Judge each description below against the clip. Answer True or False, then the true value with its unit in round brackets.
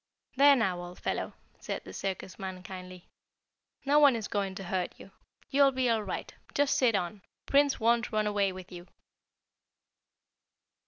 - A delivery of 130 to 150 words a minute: False (160 wpm)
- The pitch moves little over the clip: False (5.5 semitones)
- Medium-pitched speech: False (205 Hz)